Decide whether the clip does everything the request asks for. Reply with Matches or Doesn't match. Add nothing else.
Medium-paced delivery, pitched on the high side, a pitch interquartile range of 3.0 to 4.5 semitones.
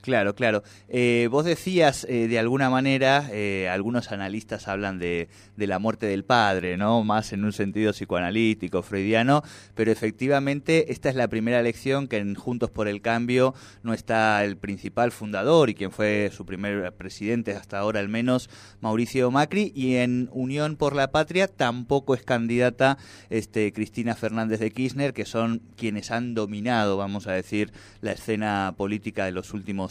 Doesn't match